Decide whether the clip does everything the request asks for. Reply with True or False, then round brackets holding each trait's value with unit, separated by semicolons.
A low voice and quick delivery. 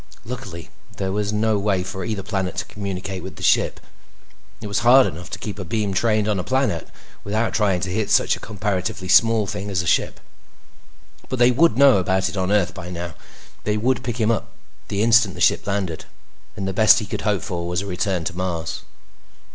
True (100 Hz; 210 wpm)